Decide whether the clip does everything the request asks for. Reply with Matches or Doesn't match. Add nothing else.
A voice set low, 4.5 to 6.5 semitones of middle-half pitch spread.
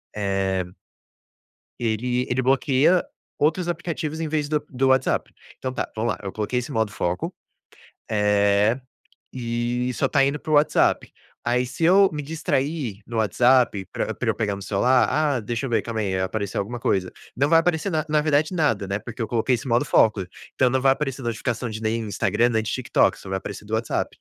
Matches